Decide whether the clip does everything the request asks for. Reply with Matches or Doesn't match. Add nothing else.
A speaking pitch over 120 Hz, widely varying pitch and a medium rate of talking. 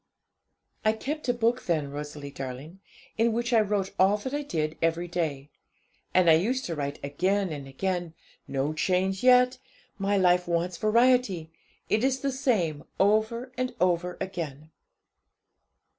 Matches